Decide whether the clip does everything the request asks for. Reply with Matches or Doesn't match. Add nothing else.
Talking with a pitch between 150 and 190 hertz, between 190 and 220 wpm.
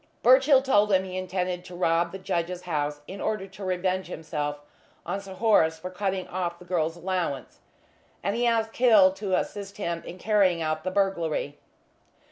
Doesn't match